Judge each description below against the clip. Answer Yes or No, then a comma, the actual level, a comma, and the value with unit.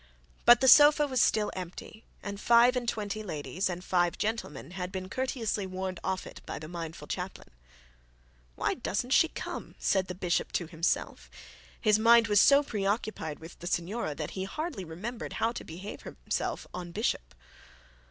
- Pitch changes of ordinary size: Yes, average, 4.9 semitones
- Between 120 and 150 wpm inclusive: No, average, 170 wpm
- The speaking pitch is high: Yes, high, 195 Hz